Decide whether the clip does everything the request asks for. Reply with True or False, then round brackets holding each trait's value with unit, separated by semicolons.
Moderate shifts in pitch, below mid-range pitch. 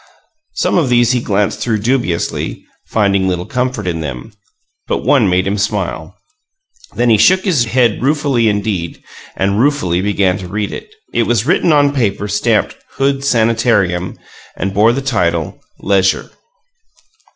True (4.5 semitones; 105 Hz)